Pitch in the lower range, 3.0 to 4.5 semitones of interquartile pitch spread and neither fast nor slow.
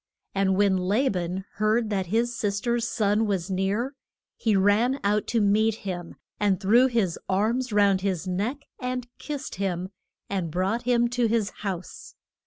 No: high, 205 Hz; average, 3.6 semitones; average, 165 wpm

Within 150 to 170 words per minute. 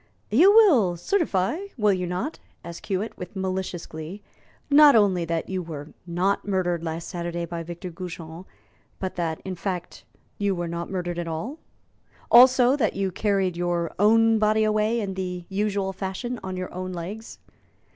Yes: average, 165 wpm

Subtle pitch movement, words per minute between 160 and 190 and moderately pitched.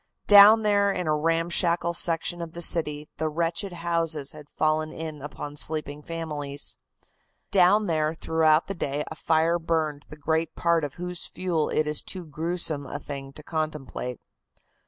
Yes: narrow, 2.1 semitones; average, 165 wpm; medium, 160 Hz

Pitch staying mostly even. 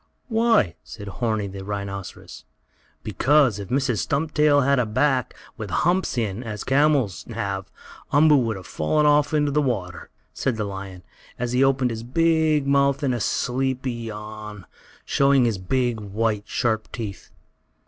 No: average, 5.0 semitones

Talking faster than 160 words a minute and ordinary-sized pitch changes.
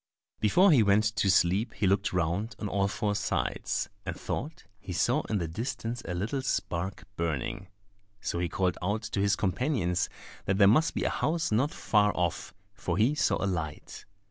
Yes: average, 185 wpm; average, 3.9 semitones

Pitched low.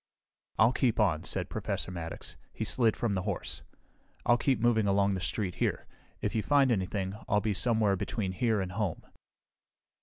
Yes: low, 105 Hz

